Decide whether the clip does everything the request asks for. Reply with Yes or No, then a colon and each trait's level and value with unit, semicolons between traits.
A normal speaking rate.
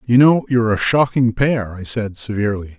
Yes: average, 195 wpm